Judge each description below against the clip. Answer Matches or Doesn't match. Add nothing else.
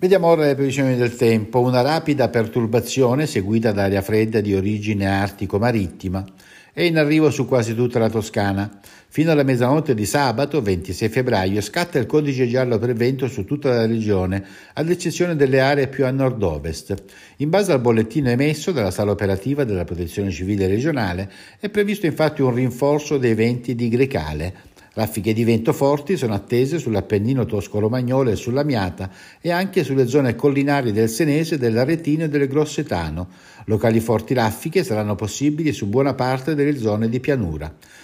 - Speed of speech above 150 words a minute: Matches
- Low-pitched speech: Matches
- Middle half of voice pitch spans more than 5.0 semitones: Matches